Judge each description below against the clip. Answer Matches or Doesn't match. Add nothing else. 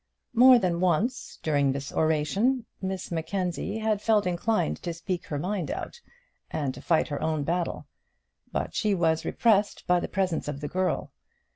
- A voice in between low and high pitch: Matches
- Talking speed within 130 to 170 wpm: Matches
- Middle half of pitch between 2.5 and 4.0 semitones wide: Doesn't match